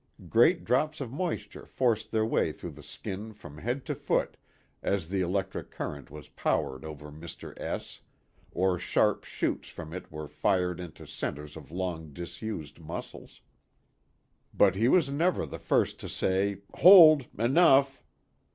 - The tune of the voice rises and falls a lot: Yes, wide, 8.0 semitones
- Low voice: Yes, very low, 95 Hz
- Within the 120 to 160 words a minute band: Yes, average, 150 wpm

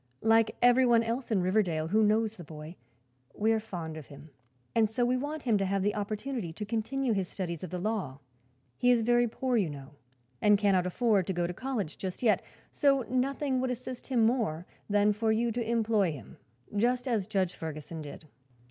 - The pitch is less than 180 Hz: No, high, 215 Hz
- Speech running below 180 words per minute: No, average, 200 wpm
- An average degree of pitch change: Yes, average, 4.8 semitones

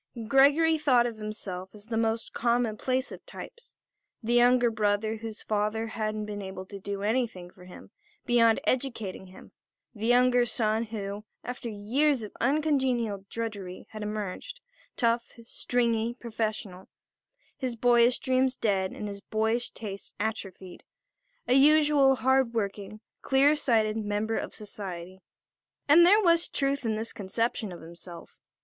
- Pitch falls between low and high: No, high, 225 Hz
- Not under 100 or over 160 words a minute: Yes, average, 140 wpm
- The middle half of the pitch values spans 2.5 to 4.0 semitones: Yes, average, 3.3 semitones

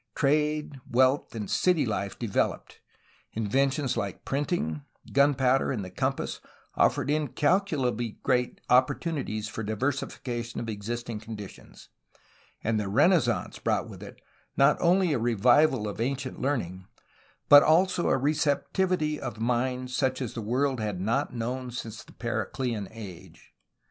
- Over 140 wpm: No, slow, 135 wpm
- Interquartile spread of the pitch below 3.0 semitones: No, average, 4.4 semitones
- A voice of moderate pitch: No, low, 125 Hz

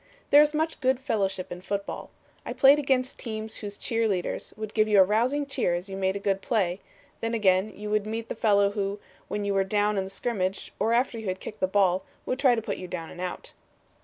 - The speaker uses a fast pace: Yes, fast, 240 wpm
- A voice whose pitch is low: No, high, 210 Hz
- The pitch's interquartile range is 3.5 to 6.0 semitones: No, average, 3.1 semitones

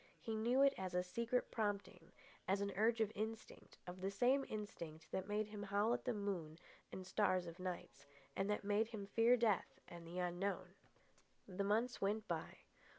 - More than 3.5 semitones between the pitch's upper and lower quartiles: No, average, 3.2 semitones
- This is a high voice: Yes, high, 200 Hz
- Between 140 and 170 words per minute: No, average, 180 wpm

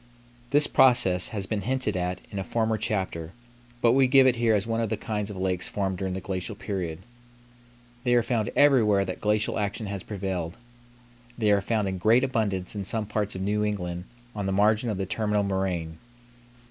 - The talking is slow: No, average, 200 wpm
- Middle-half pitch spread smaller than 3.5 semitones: Yes, average, 2.8 semitones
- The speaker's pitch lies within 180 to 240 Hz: No, low, 105 Hz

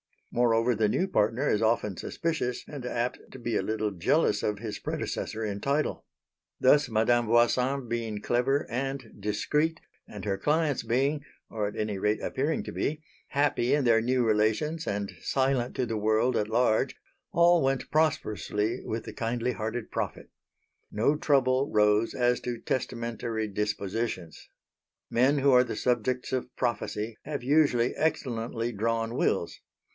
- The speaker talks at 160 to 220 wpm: No, average, 150 wpm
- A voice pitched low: Yes, low, 120 Hz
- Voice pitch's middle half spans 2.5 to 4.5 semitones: Yes, average, 3.6 semitones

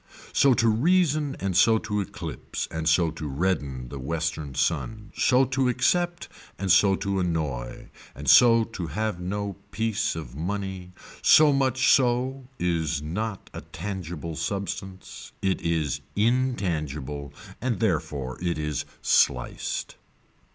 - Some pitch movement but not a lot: No, wide, 6.3 semitones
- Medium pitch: No, very low, 95 Hz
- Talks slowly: Yes, slow, 130 wpm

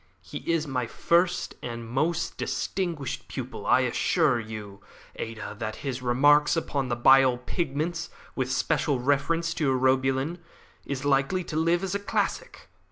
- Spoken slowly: No, average, 150 wpm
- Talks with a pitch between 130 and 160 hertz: Yes, low, 135 Hz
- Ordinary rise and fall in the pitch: Yes, average, 4.8 semitones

